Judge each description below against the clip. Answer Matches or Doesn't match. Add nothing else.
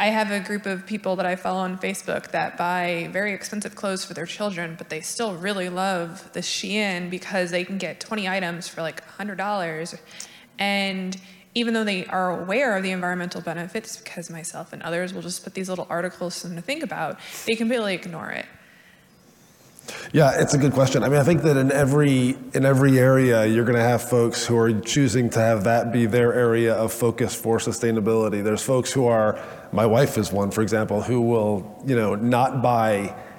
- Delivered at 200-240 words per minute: Matches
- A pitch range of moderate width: Doesn't match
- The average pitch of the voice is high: Doesn't match